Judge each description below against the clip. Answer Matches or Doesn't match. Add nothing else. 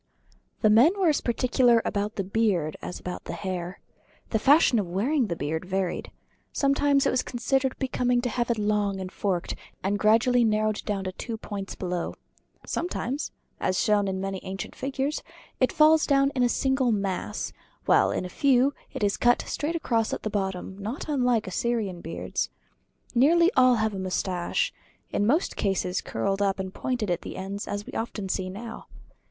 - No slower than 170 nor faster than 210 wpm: Matches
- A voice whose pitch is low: Doesn't match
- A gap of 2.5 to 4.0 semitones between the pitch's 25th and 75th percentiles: Doesn't match